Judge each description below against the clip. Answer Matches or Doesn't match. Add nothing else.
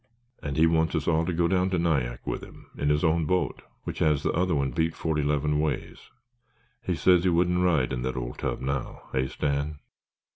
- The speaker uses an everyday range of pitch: Matches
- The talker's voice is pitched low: Matches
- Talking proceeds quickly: Matches